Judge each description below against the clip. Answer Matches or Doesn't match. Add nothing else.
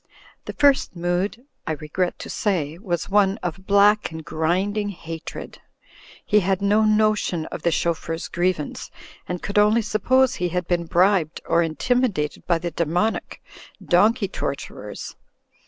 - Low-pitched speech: Doesn't match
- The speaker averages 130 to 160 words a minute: Matches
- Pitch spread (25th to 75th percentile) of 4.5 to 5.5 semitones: Doesn't match